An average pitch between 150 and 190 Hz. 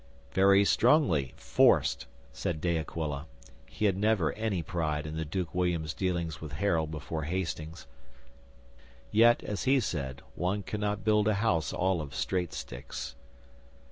No: very low, 90 Hz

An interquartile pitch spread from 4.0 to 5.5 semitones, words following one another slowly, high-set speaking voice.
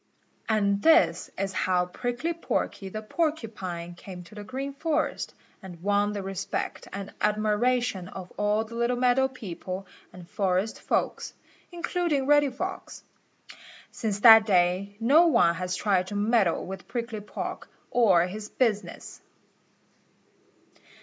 Yes: average, 4.6 semitones; slow, 130 wpm; high, 210 Hz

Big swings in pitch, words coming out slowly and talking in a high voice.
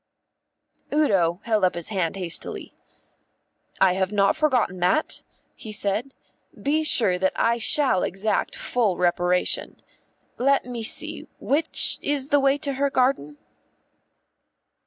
Yes: wide, 6.9 semitones; slow, 125 wpm; high, 220 Hz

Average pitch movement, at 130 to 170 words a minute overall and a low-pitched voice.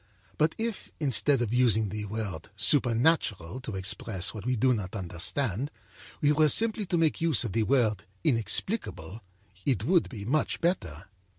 No: wide, 6.6 semitones; average, 160 wpm; low, 120 Hz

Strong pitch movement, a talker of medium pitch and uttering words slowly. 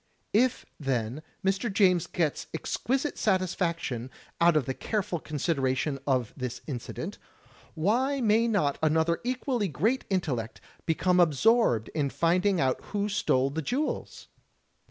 Yes: wide, 7.0 semitones; medium, 170 Hz; slow, 125 wpm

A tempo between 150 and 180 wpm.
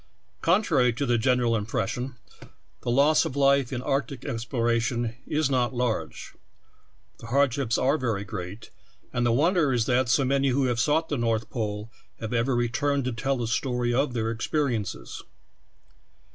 Yes: average, 160 wpm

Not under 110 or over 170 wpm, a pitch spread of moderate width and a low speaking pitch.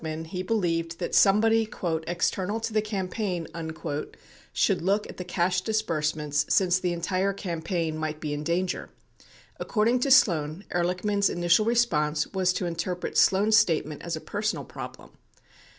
No: average, 150 wpm; average, 3.9 semitones; medium, 180 Hz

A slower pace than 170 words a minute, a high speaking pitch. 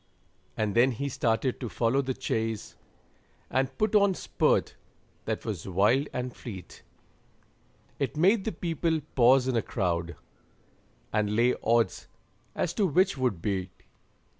No: average, 140 wpm; low, 125 Hz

